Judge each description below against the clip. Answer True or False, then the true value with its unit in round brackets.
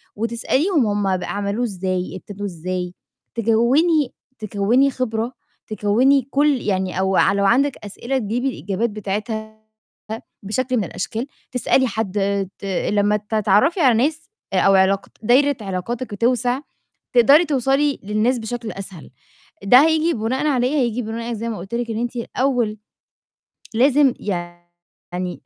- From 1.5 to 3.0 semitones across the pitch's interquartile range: False (4.4 semitones)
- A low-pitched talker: False (225 Hz)